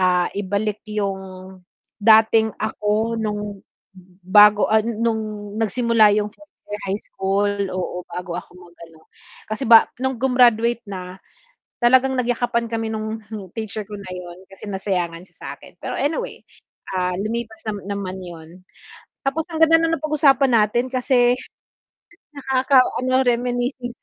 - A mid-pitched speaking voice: No, high, 220 Hz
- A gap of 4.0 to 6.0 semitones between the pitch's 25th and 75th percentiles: No, average, 3.6 semitones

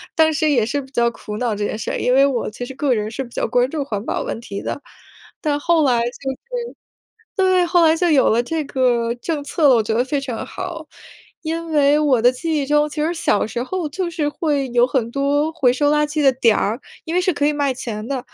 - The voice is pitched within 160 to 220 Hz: No, very high, 280 Hz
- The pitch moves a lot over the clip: No, average, 4.4 semitones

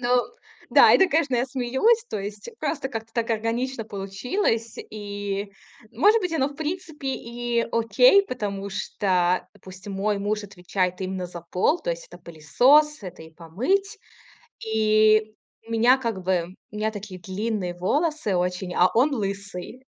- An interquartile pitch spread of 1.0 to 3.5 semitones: No, average, 5.2 semitones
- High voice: Yes, high, 215 Hz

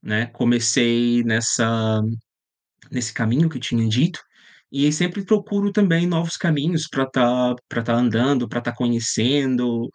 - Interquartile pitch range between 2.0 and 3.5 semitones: No, average, 5.1 semitones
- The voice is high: No, low, 125 Hz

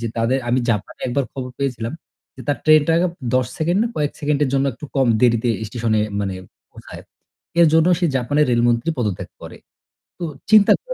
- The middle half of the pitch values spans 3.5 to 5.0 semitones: Yes, average, 4.2 semitones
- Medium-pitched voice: No, low, 130 Hz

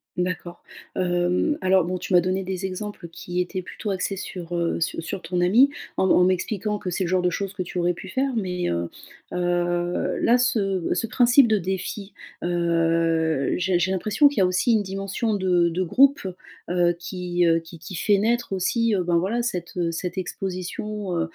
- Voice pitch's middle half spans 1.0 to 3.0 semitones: Yes, narrow, 2.4 semitones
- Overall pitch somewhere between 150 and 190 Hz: Yes, medium, 185 Hz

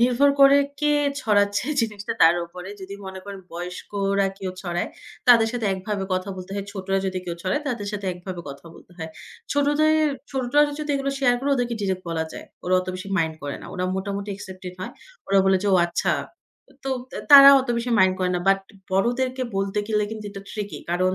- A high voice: Yes, high, 200 Hz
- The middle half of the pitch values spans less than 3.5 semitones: No, average, 4.7 semitones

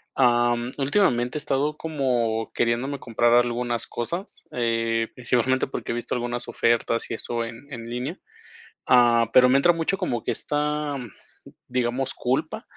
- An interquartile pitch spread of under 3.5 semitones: Yes, average, 2.8 semitones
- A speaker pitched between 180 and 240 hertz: No, low, 120 Hz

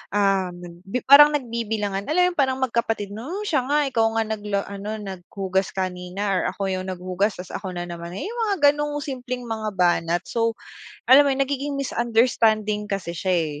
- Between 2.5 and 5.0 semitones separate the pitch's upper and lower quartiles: No, wide, 5.6 semitones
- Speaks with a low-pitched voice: No, high, 215 Hz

